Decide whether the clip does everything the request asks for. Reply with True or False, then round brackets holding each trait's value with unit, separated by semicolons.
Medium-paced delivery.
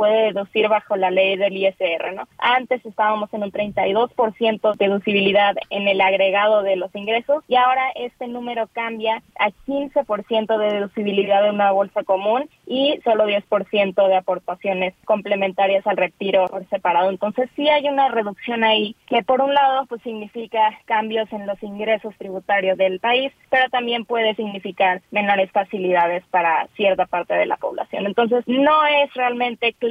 True (160 wpm)